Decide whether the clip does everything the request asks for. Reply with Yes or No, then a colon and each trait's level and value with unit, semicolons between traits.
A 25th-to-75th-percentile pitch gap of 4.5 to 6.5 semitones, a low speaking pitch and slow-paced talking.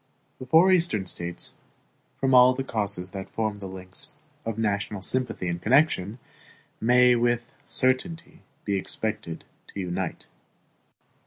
Yes: average, 5.2 semitones; low, 110 Hz; slow, 130 wpm